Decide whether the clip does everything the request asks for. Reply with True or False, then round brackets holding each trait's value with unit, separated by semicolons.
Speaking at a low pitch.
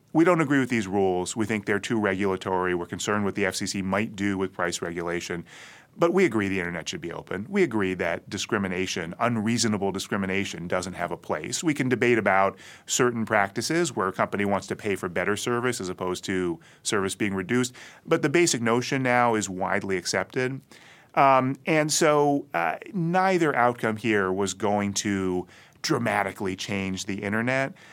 True (105 Hz)